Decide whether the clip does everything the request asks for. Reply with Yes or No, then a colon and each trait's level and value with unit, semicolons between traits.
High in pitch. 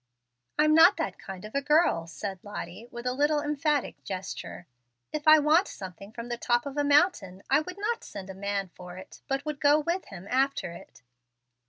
Yes: very high, 270 Hz